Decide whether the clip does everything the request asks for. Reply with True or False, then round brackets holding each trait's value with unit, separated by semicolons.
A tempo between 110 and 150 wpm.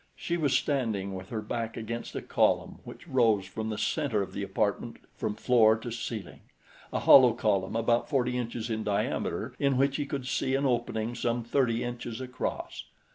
False (185 wpm)